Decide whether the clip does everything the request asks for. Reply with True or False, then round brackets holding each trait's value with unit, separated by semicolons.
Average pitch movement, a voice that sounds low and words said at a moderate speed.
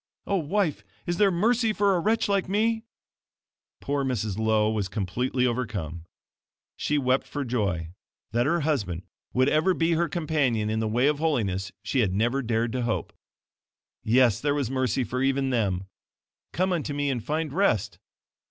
False (6.5 semitones; 130 Hz; 170 wpm)